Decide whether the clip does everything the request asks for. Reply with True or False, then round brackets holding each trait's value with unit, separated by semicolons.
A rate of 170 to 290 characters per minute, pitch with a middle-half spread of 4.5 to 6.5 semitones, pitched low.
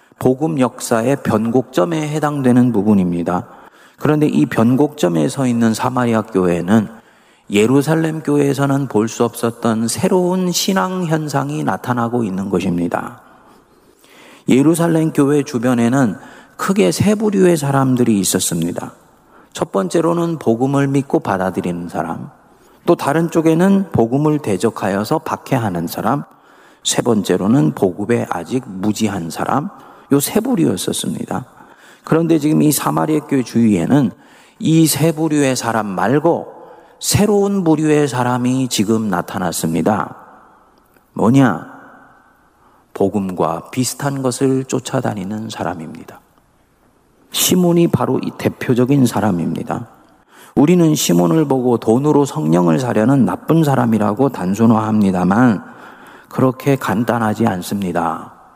True (280 characters per minute; 5.7 semitones; 130 Hz)